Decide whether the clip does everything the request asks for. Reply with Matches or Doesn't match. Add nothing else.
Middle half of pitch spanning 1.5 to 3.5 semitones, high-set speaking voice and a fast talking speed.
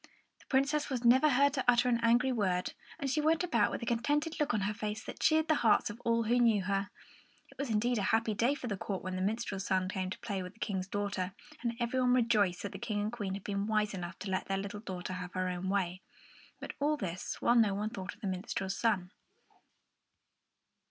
Doesn't match